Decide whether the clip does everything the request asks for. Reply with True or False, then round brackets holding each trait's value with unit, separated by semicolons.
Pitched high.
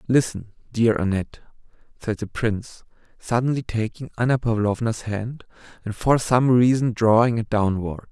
False (115 Hz)